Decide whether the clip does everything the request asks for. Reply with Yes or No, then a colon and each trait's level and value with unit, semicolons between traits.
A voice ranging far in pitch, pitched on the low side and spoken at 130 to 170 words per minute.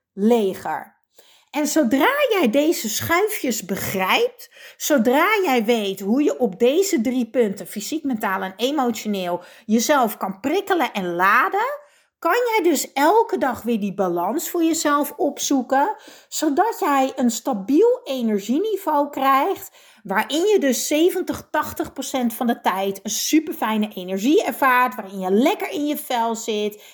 No: wide, 6.5 semitones; very high, 265 Hz; average, 140 wpm